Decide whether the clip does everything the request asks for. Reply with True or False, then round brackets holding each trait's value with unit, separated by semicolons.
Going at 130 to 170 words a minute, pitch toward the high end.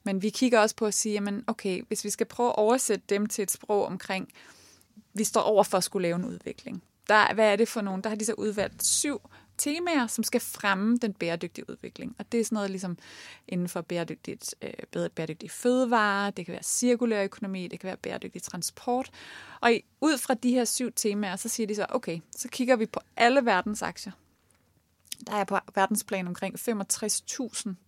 False (200 wpm; 210 Hz)